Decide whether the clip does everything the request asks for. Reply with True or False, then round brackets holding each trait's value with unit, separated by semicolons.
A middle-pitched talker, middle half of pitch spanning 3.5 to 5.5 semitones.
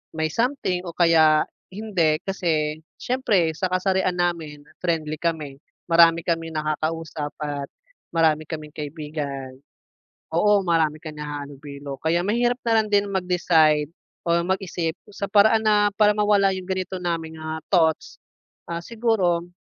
True (170 Hz; 3.8 semitones)